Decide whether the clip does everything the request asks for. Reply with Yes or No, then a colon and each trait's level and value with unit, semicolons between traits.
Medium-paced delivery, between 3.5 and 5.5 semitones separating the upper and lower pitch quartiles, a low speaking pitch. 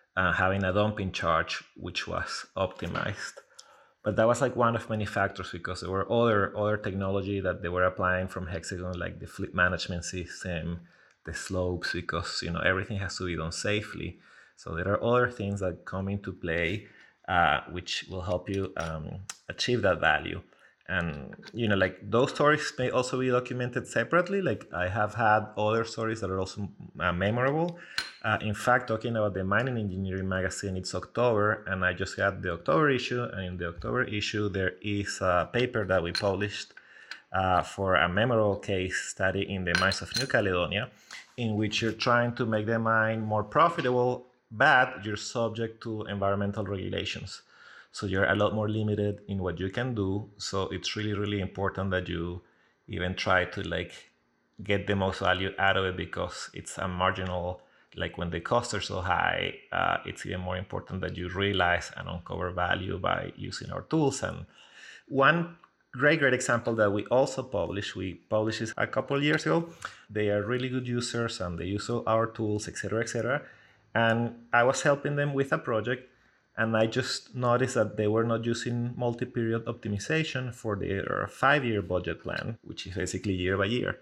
Yes: average, 185 wpm; average, 3.9 semitones; low, 105 Hz